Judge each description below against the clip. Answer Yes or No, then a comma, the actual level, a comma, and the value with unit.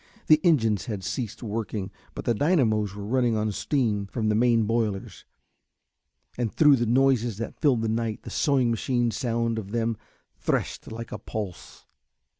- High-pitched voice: No, low, 115 Hz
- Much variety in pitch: No, narrow, 2.4 semitones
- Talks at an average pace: Yes, average, 165 wpm